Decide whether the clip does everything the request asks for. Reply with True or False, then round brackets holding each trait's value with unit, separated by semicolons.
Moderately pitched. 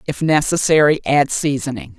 True (145 Hz)